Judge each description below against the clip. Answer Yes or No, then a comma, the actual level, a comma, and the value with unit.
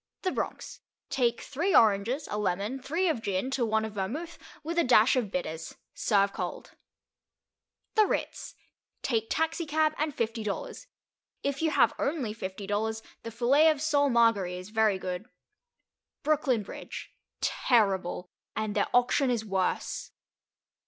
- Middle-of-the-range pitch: No, high, 230 Hz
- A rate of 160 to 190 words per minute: No, average, 145 wpm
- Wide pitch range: Yes, wide, 5.9 semitones